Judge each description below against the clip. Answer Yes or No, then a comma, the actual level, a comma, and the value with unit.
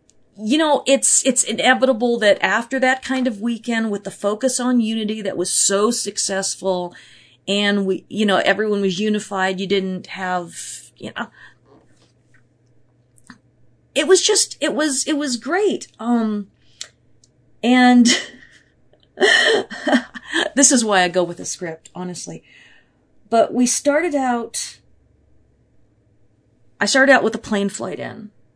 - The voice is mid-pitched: No, high, 215 Hz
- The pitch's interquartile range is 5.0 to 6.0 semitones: Yes, wide, 5.4 semitones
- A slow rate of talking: Yes, slow, 130 wpm